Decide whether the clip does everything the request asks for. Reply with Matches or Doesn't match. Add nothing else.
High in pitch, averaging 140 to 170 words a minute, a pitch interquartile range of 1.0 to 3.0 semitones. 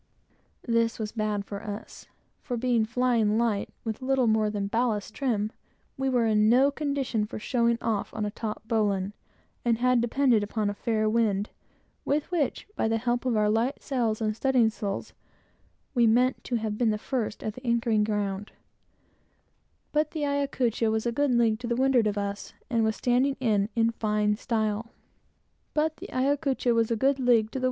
Matches